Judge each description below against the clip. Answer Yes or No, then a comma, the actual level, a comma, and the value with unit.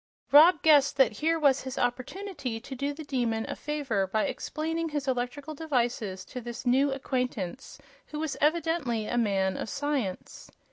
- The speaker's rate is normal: Yes, average, 160 wpm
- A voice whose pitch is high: Yes, very high, 270 Hz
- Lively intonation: No, average, 4.2 semitones